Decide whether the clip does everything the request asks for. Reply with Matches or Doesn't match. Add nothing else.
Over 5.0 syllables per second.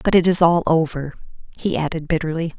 Matches